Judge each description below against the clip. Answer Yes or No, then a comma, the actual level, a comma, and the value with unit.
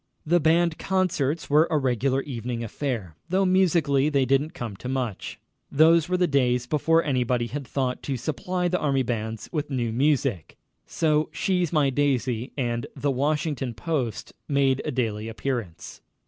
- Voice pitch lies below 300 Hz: Yes, medium, 140 Hz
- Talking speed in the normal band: Yes, average, 160 wpm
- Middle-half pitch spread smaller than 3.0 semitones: No, average, 4.1 semitones